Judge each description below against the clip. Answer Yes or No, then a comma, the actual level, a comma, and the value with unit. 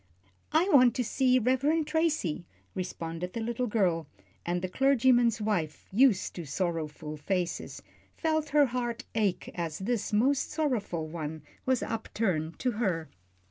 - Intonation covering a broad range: Yes, wide, 7.0 semitones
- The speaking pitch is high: Yes, high, 220 Hz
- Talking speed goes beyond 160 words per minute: No, average, 140 wpm